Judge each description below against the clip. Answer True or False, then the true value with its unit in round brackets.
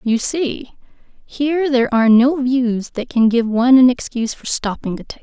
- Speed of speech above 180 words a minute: True (205 wpm)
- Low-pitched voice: False (250 Hz)